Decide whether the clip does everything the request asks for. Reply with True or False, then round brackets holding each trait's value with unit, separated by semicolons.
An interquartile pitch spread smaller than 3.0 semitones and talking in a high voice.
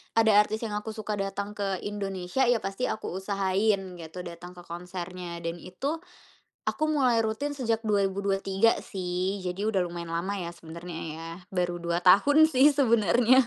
False (3.7 semitones; 195 Hz)